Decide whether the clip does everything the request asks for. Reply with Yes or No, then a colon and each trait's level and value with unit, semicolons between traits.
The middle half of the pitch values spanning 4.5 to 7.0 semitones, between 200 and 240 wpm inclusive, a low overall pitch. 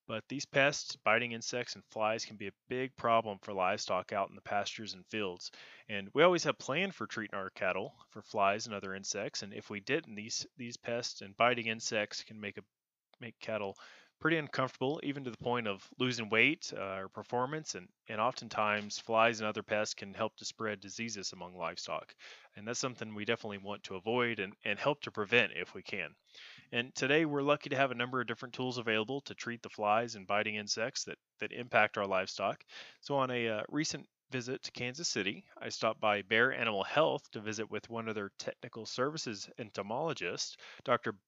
No: average, 3.3 semitones; fast, 205 wpm; low, 115 Hz